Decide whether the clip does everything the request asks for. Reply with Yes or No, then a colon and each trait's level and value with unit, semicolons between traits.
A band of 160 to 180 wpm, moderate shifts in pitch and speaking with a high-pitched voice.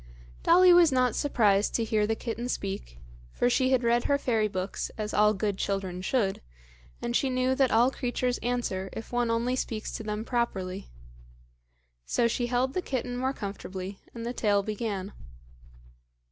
Yes: average, 170 wpm; average, 3.6 semitones; high, 230 Hz